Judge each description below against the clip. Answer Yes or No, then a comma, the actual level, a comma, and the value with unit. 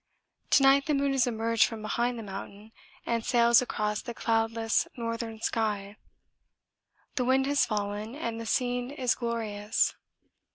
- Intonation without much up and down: Yes, narrow, 2.2 semitones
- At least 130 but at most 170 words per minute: Yes, average, 150 wpm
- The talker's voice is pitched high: Yes, high, 230 Hz